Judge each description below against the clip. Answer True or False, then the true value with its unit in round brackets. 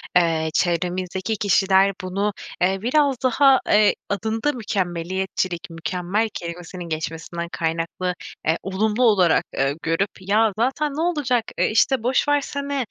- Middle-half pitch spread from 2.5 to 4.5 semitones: False (5.1 semitones)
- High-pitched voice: True (195 Hz)